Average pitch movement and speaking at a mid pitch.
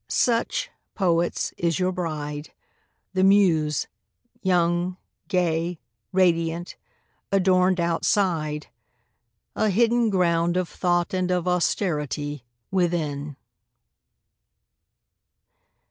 No: narrow, 2.2 semitones; medium, 175 Hz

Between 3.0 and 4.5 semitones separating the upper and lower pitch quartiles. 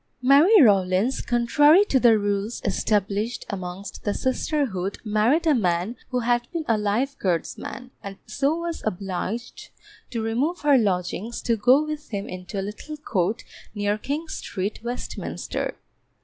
No: wide, 5.5 semitones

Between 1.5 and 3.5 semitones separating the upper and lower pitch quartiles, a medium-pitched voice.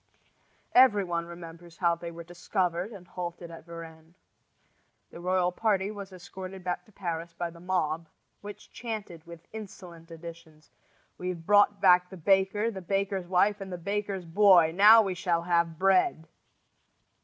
Yes: narrow, 2.6 semitones; medium, 180 Hz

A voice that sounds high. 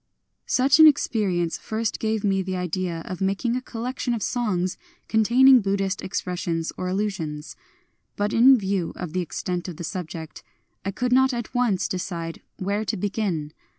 Yes: high, 195 Hz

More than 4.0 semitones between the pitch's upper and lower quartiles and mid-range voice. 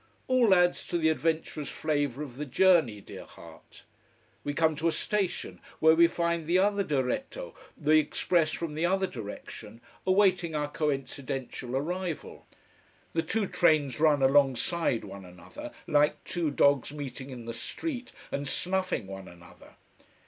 Yes: average, 4.6 semitones; medium, 155 Hz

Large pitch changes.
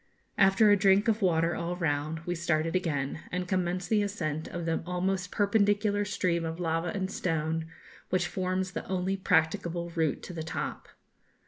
No: average, 2.8 semitones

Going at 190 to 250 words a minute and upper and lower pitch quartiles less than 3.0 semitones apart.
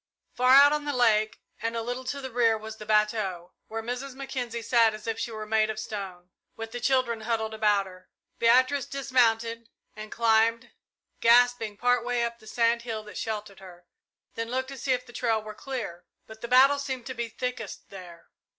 Yes: average, 200 wpm; narrow, 2.4 semitones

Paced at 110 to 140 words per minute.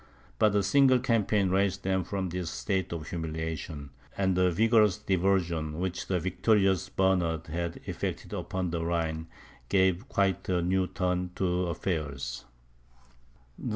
Yes: slow, 135 wpm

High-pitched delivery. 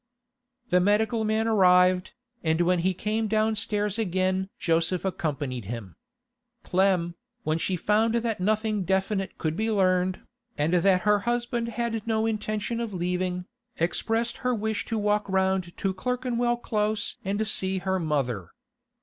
Yes: high, 195 Hz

